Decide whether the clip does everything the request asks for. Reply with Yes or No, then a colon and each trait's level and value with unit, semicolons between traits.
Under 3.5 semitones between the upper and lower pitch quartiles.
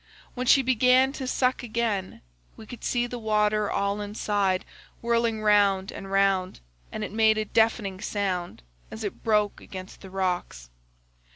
Yes: average, 3.0 semitones